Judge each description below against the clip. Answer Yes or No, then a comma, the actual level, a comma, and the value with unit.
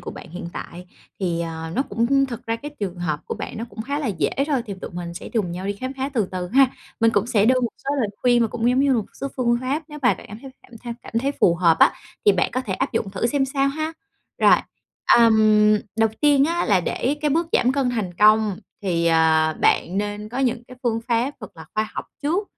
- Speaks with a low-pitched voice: No, high, 230 Hz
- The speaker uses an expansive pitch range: Yes, wide, 5.7 semitones